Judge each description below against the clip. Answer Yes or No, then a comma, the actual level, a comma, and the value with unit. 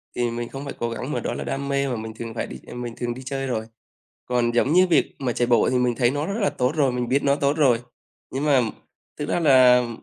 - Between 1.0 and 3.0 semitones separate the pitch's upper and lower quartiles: Yes, narrow, 2.6 semitones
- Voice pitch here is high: No, low, 125 Hz